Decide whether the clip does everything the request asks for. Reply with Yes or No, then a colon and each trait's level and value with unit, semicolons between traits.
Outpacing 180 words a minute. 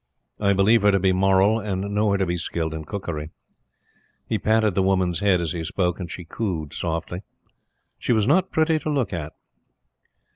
Yes: average, 190 wpm